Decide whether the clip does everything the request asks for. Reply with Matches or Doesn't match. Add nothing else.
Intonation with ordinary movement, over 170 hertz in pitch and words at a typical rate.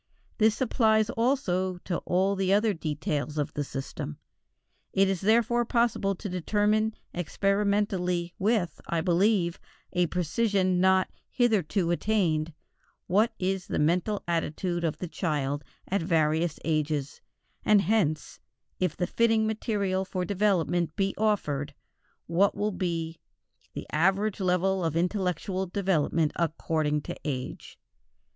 Doesn't match